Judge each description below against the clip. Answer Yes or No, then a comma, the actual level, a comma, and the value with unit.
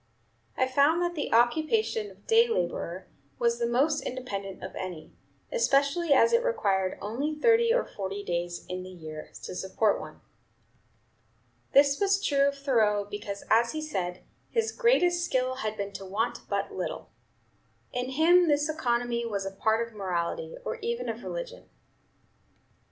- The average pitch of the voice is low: No, very high, 255 Hz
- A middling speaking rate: Yes, average, 155 wpm